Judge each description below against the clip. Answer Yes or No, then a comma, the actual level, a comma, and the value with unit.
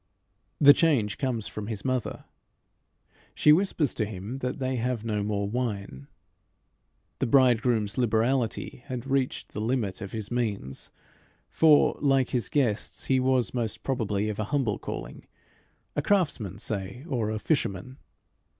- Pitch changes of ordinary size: Yes, average, 3.9 semitones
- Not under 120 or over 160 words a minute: Yes, average, 140 wpm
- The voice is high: No, low, 120 Hz